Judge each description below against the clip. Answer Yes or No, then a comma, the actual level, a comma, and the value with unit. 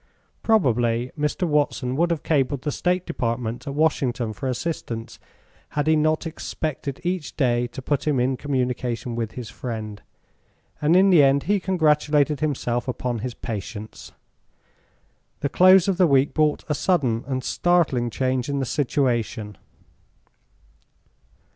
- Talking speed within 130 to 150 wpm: Yes, average, 140 wpm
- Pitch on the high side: No, low, 135 Hz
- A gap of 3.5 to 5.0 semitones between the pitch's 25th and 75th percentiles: Yes, average, 4.2 semitones